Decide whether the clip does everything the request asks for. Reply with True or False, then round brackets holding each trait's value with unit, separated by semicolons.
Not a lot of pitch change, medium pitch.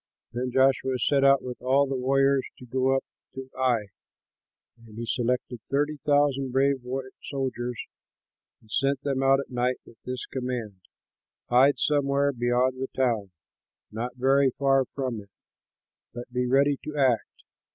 False (1.8 semitones; 130 Hz)